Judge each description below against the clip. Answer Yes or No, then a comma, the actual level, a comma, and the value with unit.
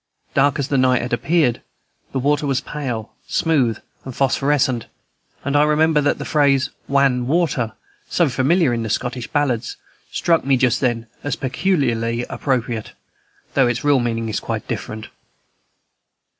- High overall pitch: No, low, 135 Hz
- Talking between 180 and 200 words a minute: No, average, 150 wpm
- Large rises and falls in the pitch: No, average, 3.2 semitones